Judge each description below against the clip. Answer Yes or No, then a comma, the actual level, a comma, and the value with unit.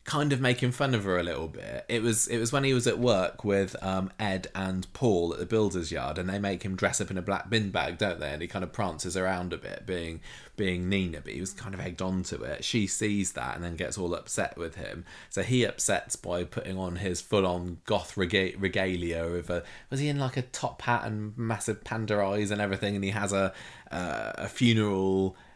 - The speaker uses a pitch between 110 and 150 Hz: No, very low, 95 Hz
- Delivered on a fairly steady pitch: No, average, 3.5 semitones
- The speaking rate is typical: No, fast, 245 wpm